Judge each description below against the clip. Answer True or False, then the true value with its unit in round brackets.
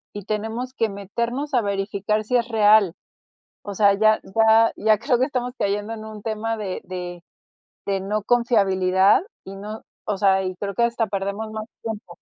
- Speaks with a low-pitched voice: False (215 Hz)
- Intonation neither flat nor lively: False (2.3 semitones)